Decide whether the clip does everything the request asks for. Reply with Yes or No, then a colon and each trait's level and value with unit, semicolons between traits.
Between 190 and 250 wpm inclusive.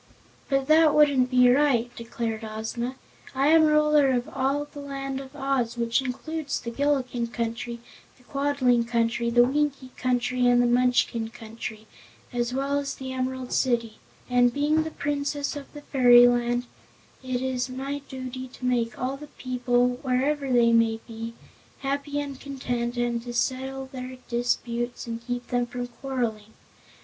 No: average, 155 wpm